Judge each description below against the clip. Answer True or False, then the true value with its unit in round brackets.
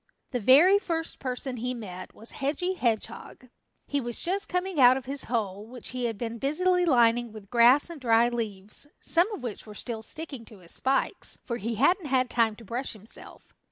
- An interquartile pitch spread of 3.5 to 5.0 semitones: True (4.1 semitones)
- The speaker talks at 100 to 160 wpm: False (195 wpm)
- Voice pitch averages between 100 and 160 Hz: False (245 Hz)